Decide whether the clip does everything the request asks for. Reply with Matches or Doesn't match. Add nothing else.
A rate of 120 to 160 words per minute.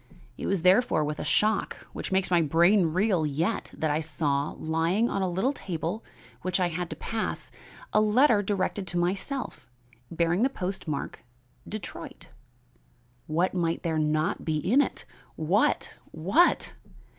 Matches